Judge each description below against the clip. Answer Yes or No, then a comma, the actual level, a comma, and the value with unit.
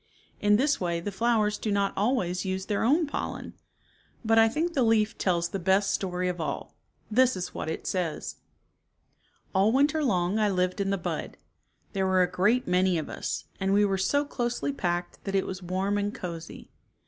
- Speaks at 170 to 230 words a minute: Yes, average, 195 wpm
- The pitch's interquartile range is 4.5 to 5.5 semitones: No, average, 3.6 semitones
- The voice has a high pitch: Yes, high, 195 Hz